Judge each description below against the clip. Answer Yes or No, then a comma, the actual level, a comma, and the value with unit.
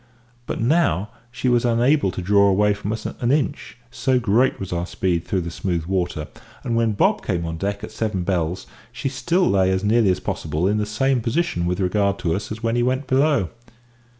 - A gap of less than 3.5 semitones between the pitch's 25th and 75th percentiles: No, average, 4.7 semitones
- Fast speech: Yes, fast, 210 wpm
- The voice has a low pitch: Yes, low, 105 Hz